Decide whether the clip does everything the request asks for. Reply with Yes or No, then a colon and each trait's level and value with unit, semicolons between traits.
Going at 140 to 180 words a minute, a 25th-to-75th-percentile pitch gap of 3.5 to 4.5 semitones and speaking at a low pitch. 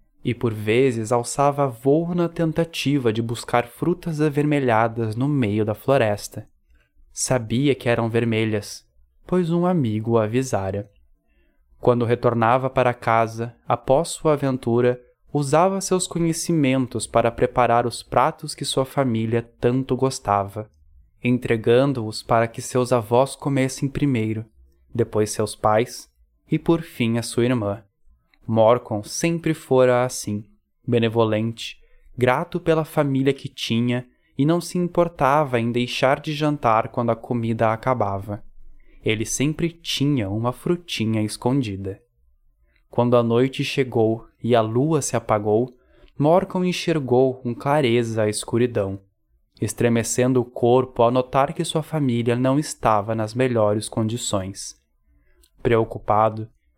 No: average, 125 wpm; average, 3.9 semitones; low, 120 Hz